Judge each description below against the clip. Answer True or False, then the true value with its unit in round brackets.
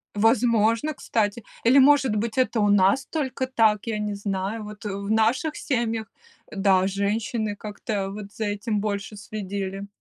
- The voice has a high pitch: True (210 Hz)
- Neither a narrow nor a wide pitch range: False (2.3 semitones)